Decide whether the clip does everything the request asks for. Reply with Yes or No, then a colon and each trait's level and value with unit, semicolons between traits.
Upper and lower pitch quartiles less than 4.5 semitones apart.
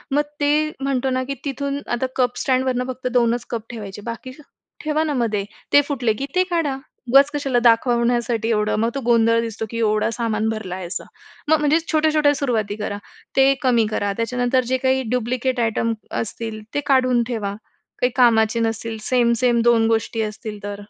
Yes: average, 2.8 semitones